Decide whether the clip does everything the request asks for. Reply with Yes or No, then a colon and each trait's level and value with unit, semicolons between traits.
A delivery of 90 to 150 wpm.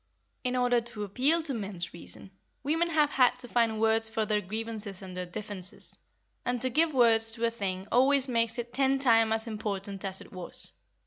No: average, 195 wpm